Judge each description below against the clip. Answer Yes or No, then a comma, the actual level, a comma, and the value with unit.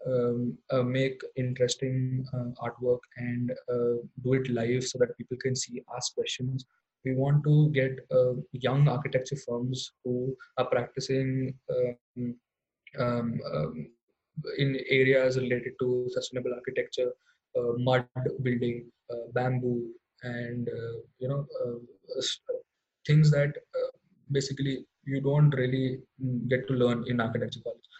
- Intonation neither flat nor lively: No, narrow, 1.7 semitones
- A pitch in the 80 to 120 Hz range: No, low, 130 Hz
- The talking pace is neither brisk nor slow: No, slow, 130 wpm